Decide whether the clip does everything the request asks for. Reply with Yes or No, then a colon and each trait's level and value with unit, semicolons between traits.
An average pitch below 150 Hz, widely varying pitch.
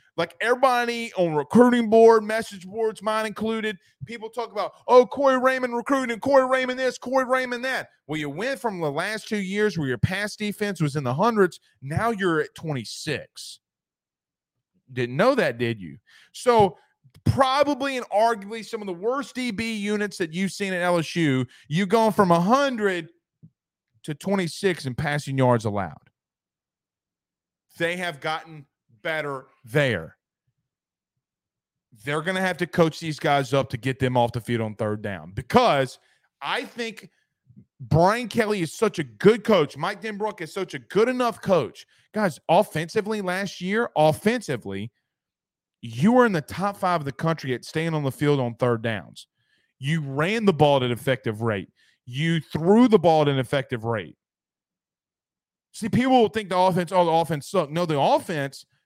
No: medium, 175 Hz; wide, 7.6 semitones